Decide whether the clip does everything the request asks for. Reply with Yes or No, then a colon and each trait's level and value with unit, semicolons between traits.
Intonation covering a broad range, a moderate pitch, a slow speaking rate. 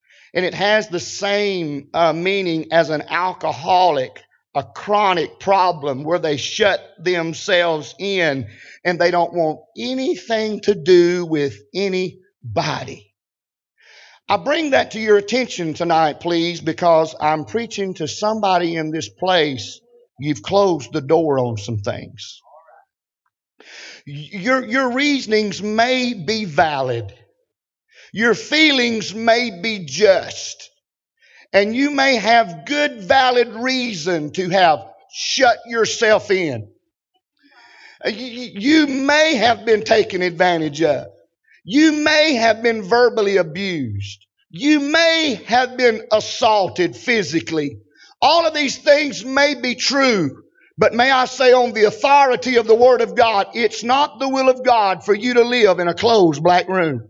No: wide, 6.8 semitones; high, 200 Hz; slow, 130 wpm